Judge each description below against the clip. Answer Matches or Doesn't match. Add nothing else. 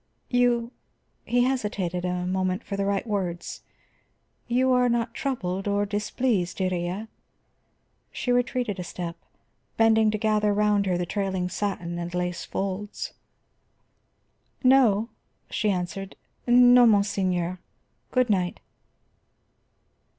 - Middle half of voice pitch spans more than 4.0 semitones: Matches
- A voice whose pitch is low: Doesn't match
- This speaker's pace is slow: Matches